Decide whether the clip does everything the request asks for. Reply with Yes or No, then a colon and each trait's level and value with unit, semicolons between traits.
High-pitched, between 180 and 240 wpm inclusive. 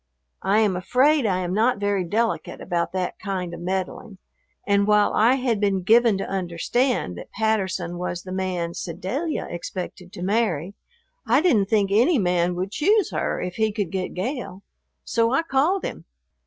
No: high, 200 Hz; average, 170 wpm